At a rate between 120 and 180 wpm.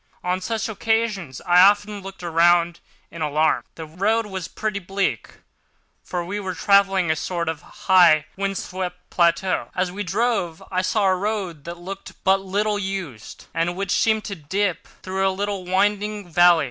Yes: average, 170 wpm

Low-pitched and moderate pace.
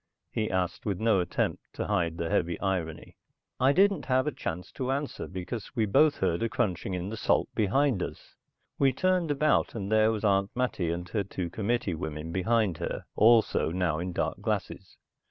Yes: low, 100 Hz; average, 190 wpm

